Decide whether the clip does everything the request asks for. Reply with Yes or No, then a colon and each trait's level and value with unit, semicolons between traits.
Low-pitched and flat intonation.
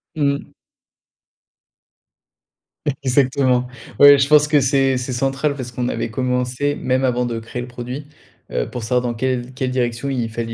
Yes: low, 130 Hz; narrow, 1.9 semitones